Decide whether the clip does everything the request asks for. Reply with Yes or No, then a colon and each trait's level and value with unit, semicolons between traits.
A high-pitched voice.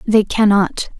Yes: high, 205 Hz